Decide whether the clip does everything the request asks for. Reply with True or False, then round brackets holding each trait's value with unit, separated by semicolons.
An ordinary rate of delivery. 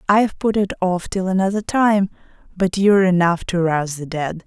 True (190 wpm)